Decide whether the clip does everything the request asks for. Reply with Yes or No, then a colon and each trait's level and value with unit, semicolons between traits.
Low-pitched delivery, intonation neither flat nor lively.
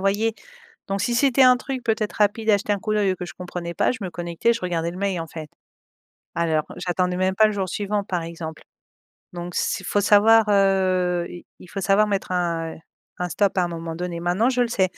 No: high, 190 Hz; average, 3.2 semitones